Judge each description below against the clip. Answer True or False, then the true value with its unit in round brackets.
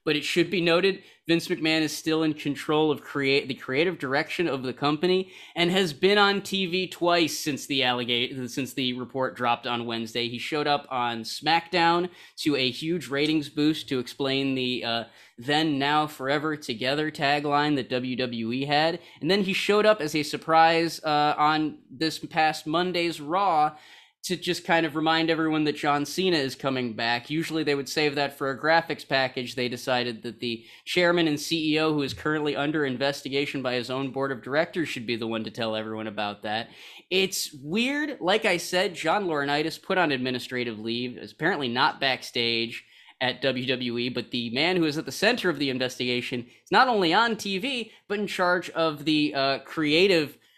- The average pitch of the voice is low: False (150 Hz)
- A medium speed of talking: True (185 wpm)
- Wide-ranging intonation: False (4.4 semitones)